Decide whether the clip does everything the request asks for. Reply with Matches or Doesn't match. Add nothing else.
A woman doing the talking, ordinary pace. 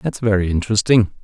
Doesn't match